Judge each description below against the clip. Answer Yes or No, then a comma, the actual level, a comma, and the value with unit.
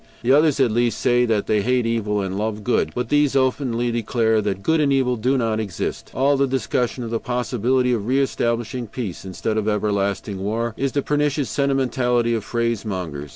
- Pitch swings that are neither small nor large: Yes, average, 3.4 semitones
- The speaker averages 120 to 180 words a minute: No, average, 190 wpm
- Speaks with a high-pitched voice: No, low, 120 Hz